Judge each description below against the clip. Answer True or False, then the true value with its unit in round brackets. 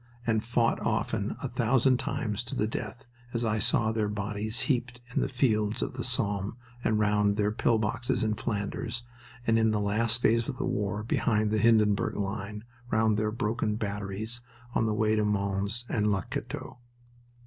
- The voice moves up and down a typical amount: False (2.0 semitones)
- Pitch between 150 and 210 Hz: False (110 Hz)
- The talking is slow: False (180 wpm)